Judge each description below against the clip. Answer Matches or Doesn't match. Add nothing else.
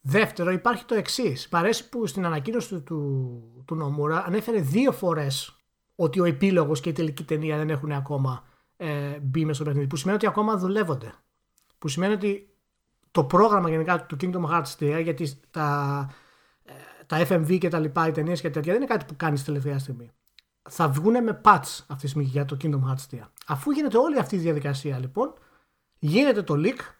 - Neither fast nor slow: Doesn't match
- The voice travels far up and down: Doesn't match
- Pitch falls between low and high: Matches